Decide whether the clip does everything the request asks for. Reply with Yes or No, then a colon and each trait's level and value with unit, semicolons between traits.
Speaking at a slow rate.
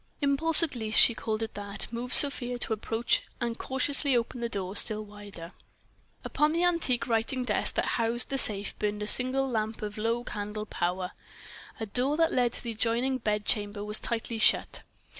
No: average, 180 wpm